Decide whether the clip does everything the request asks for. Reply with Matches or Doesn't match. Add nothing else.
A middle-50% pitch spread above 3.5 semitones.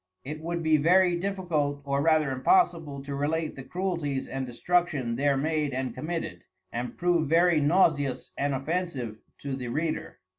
Matches